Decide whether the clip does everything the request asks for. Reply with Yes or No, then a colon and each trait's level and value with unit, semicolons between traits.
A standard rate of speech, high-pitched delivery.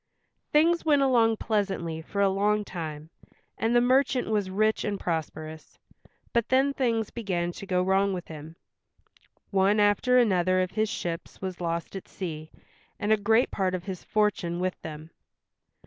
Yes: average, 165 wpm; high, 195 Hz